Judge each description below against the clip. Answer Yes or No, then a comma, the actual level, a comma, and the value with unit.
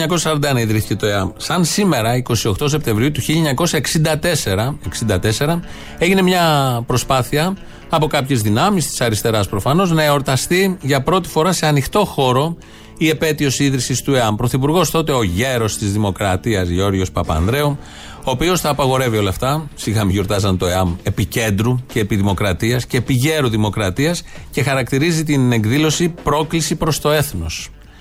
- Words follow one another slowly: No, average, 135 wpm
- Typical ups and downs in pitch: No, wide, 6.3 semitones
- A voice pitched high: No, low, 135 Hz